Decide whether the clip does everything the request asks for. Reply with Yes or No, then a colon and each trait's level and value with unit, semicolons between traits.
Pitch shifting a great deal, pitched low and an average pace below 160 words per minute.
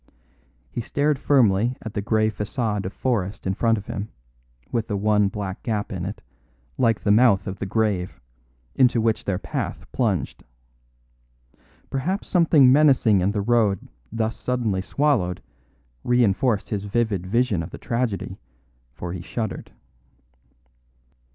No: average, 3.7 semitones; low, 110 Hz; average, 140 wpm